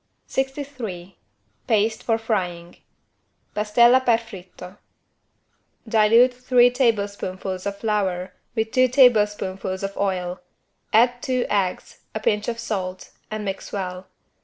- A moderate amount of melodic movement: Yes, average, 4.0 semitones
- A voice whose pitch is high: Yes, high, 210 Hz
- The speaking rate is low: Yes, slow, 110 wpm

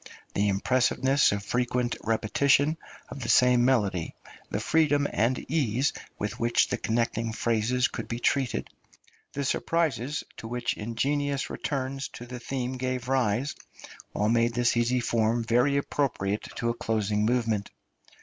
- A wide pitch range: No, average, 2.9 semitones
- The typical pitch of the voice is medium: No, low, 120 Hz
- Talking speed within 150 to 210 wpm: No, average, 140 wpm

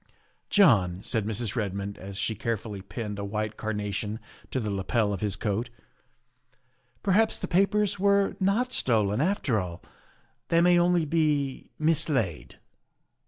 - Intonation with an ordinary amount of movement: No, wide, 8.3 semitones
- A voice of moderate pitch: No, low, 115 Hz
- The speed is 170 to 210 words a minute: No, average, 155 wpm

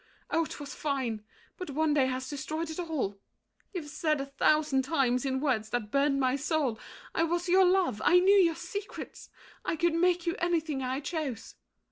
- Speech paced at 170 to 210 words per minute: Yes, average, 180 wpm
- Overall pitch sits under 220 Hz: No, very high, 300 Hz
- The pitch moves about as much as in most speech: Yes, average, 4.3 semitones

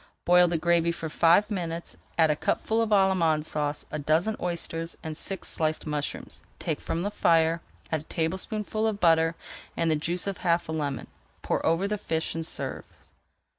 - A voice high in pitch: No, medium, 165 Hz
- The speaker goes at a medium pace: Yes, average, 190 wpm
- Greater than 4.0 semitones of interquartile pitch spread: No, narrow, 2.6 semitones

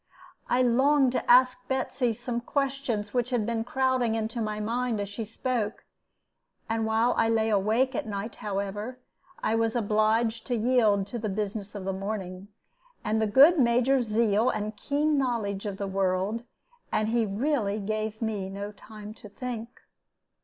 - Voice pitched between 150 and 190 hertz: No, high, 220 Hz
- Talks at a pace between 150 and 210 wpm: Yes, average, 165 wpm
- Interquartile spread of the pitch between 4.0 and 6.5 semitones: No, average, 2.9 semitones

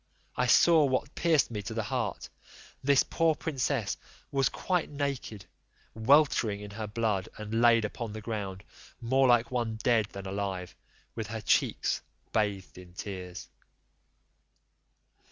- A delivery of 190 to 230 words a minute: No, slow, 135 wpm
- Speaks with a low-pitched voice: Yes, low, 115 Hz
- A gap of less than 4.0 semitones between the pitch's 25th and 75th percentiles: No, average, 4.4 semitones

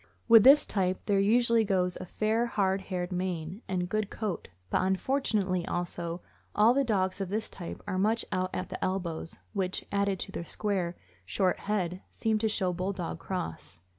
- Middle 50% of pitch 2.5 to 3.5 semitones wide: Yes, average, 2.9 semitones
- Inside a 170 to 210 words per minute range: Yes, average, 175 wpm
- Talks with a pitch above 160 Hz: Yes, high, 190 Hz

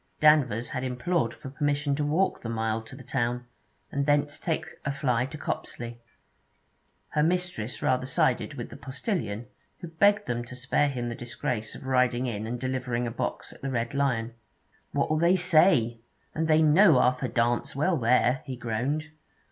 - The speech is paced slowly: No, average, 175 wpm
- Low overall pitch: Yes, low, 130 Hz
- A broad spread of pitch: No, average, 4.1 semitones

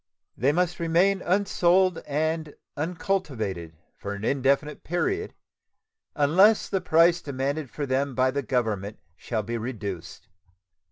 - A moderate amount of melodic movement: No, wide, 6.4 semitones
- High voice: No, medium, 145 Hz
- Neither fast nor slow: No, slow, 120 wpm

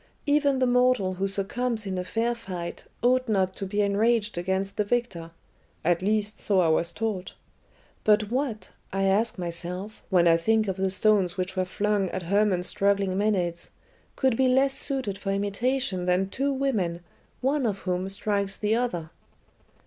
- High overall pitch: Yes, high, 200 Hz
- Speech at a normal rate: Yes, average, 170 wpm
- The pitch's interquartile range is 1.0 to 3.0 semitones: No, average, 3.7 semitones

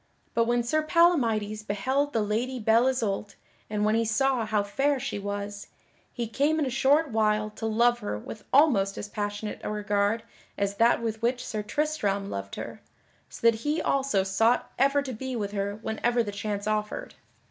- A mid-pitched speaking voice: No, high, 220 Hz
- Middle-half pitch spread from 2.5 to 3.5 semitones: No, average, 4.1 semitones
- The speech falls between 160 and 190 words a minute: Yes, average, 185 wpm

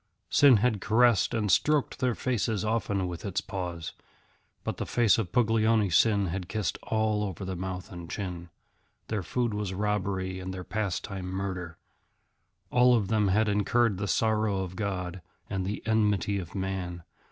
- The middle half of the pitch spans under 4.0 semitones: Yes, average, 2.9 semitones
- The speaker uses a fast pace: No, average, 165 wpm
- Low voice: Yes, low, 100 Hz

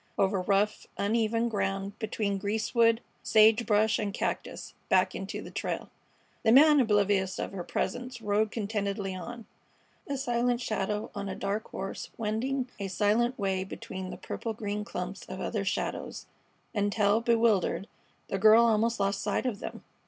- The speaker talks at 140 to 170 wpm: Yes, average, 150 wpm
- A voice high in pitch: Yes, high, 210 Hz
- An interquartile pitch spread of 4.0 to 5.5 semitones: No, narrow, 2.6 semitones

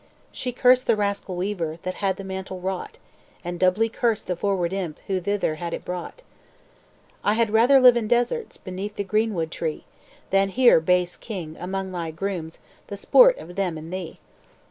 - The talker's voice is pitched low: No, high, 190 Hz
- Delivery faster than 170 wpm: Yes, average, 180 wpm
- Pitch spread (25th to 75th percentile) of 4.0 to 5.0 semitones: No, average, 3.4 semitones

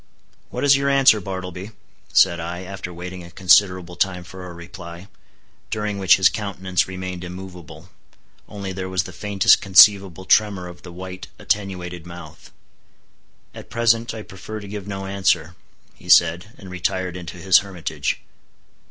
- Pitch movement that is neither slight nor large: No, narrow, 2.0 semitones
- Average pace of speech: Yes, average, 150 wpm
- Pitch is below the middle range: Yes, very low, 95 Hz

